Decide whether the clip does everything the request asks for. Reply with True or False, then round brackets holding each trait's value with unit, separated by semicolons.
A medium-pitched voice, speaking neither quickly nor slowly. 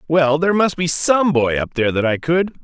False (155 Hz; 250 wpm)